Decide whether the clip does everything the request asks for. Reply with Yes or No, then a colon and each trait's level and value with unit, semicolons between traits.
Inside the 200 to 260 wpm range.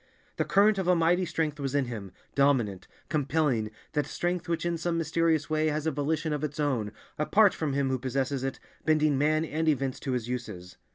Yes: fast, 205 wpm